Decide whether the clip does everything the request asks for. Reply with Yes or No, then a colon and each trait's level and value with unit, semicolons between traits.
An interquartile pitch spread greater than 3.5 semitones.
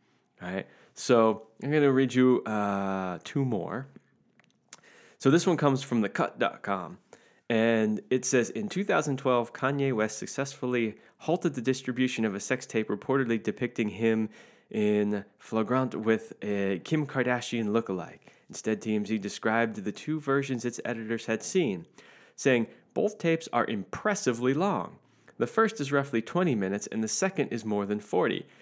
Yes: average, 4.2 semitones